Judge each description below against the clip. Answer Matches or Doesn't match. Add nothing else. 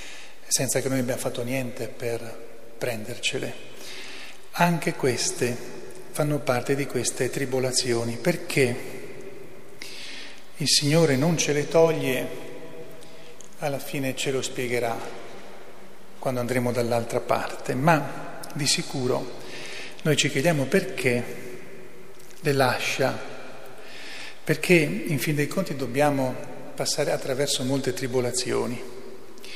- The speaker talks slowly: Matches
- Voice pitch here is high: Doesn't match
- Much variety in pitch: Doesn't match